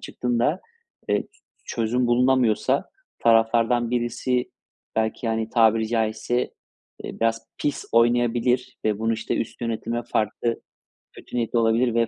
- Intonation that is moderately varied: No, narrow, 1.4 semitones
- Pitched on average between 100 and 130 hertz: Yes, low, 115 Hz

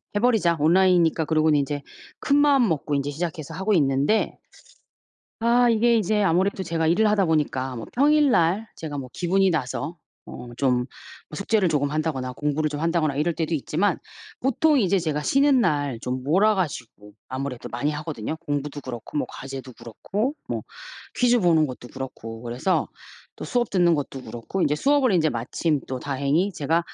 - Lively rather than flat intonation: Yes, wide, 5.8 semitones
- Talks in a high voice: No, medium, 160 Hz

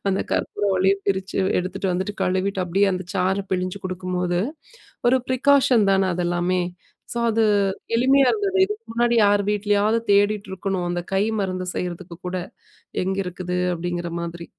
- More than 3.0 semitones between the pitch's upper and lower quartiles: No, narrow, 2.4 semitones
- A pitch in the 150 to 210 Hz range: Yes, high, 190 Hz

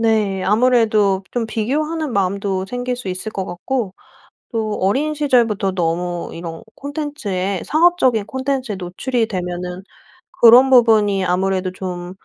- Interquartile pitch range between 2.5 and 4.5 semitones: No, average, 5.1 semitones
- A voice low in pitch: No, high, 210 Hz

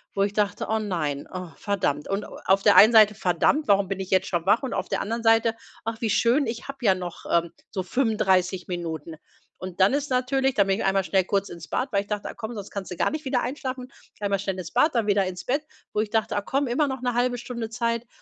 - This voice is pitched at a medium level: No, high, 210 Hz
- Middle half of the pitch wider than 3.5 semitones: Yes, average, 4.3 semitones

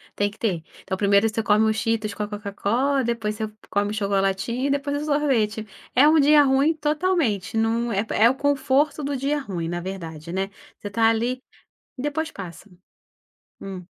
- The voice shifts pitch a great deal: Yes, wide, 5.7 semitones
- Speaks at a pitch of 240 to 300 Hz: No, high, 225 Hz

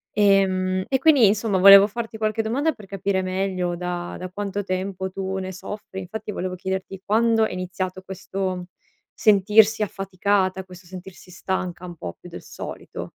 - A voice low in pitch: No, high, 190 Hz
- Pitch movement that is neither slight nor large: No, narrow, 1.9 semitones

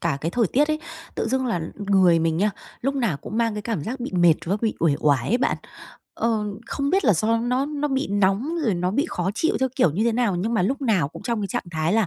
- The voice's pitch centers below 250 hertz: Yes, high, 220 Hz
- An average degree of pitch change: No, wide, 5.8 semitones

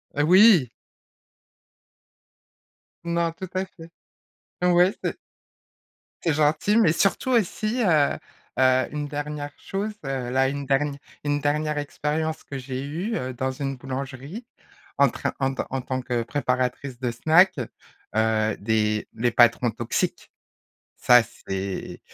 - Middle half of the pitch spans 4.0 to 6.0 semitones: Yes, average, 4.4 semitones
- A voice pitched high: No, medium, 140 Hz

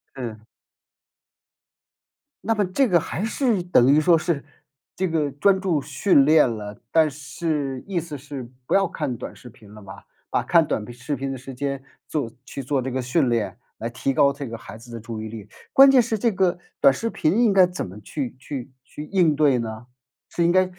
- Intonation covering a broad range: Yes, wide, 6.1 semitones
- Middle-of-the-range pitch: Yes, medium, 145 Hz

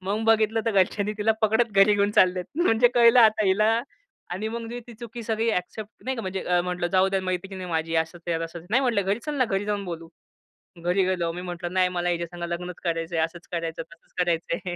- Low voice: No, high, 190 Hz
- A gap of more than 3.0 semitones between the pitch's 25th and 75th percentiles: Yes, average, 3.9 semitones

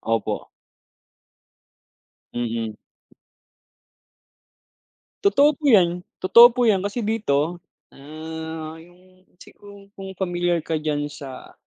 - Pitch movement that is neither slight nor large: Yes, average, 4.6 semitones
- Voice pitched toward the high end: No, medium, 175 Hz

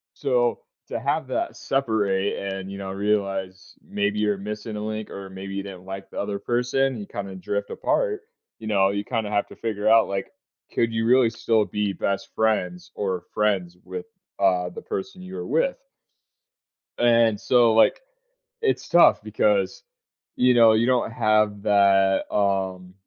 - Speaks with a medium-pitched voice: No, low, 105 Hz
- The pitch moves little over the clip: No, average, 3.1 semitones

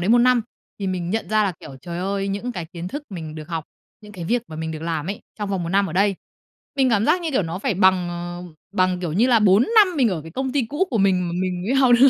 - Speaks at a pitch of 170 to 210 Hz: Yes, high, 195 Hz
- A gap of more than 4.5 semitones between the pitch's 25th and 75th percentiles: Yes, average, 5.1 semitones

